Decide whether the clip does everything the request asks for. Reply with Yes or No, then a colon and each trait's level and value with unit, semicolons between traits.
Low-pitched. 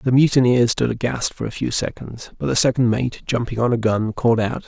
Yes: low, 120 Hz